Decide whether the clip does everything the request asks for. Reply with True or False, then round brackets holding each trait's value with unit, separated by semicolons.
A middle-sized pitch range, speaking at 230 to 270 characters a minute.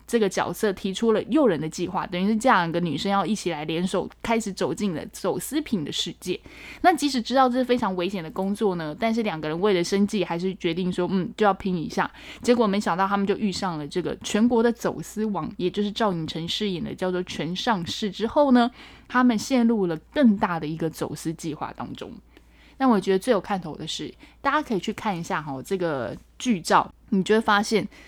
False (4.5 semitones; 325 characters per minute)